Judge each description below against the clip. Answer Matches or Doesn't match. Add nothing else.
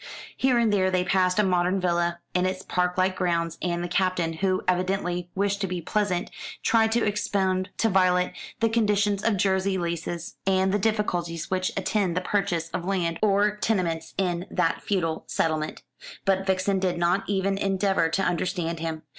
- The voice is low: Doesn't match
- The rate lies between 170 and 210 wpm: Matches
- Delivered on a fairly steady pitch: Matches